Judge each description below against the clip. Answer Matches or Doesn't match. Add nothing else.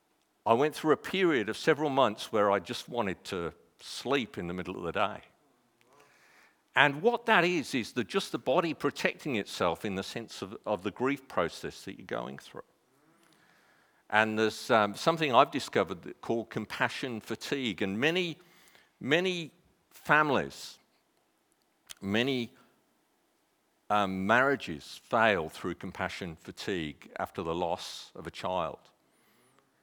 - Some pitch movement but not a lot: Doesn't match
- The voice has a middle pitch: Doesn't match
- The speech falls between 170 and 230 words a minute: Doesn't match